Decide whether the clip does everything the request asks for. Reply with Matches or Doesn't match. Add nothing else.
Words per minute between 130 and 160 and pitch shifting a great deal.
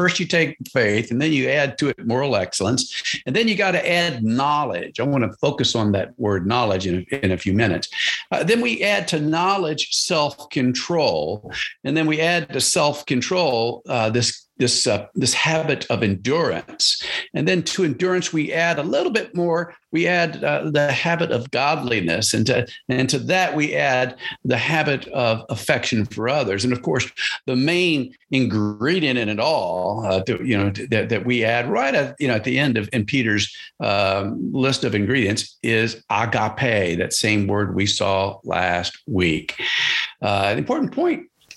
Doesn't match